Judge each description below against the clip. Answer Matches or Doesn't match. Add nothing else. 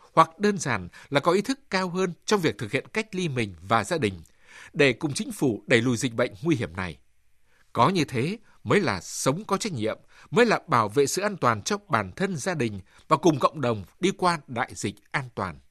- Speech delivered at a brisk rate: Doesn't match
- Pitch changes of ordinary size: Doesn't match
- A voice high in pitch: Doesn't match